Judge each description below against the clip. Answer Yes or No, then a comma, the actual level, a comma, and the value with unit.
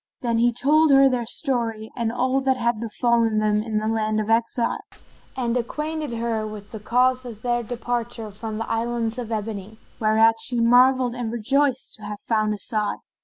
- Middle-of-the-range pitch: No, high, 235 Hz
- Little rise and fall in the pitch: Yes, narrow, 2.2 semitones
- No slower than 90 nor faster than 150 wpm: No, average, 180 wpm